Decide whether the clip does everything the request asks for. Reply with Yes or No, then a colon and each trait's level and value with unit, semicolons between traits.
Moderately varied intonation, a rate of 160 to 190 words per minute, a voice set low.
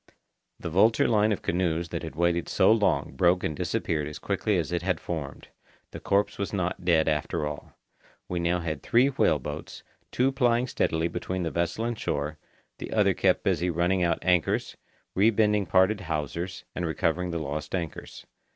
Yes: average, 3.5 semitones; average, 180 wpm; very low, 85 Hz